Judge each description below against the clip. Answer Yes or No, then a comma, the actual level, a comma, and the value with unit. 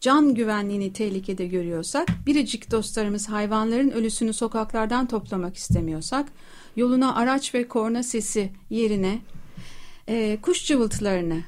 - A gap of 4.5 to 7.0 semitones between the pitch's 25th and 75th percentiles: No, average, 3.8 semitones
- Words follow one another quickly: No, average, 105 wpm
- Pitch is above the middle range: Yes, high, 220 Hz